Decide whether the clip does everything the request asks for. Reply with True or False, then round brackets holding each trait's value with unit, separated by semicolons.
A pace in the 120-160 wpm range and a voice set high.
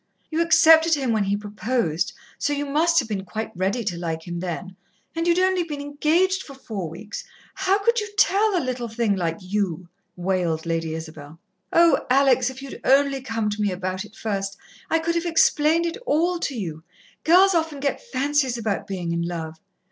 False (195 wpm; 240 Hz)